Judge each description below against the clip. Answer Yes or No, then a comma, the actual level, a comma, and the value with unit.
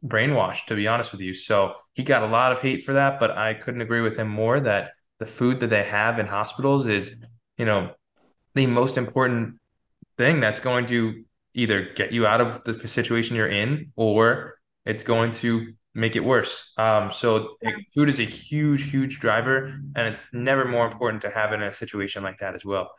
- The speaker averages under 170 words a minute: No, fast, 205 wpm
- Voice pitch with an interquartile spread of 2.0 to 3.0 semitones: Yes, average, 2.7 semitones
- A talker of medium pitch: No, low, 115 Hz